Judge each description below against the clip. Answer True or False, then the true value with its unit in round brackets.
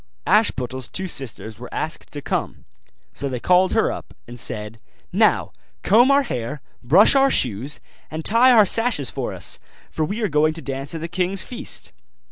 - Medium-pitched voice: True (155 Hz)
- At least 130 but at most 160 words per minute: False (180 wpm)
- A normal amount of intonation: False (7.7 semitones)